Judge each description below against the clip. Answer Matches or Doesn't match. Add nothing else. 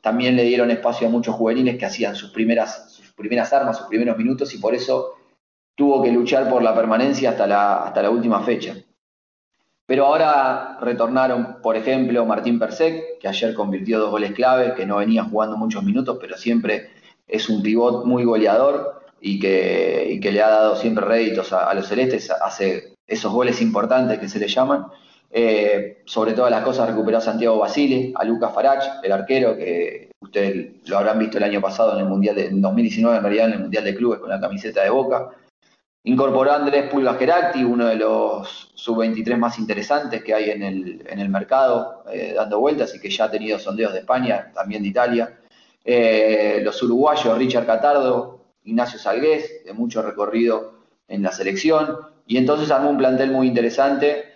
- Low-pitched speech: Matches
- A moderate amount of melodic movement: Matches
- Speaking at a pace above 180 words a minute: Matches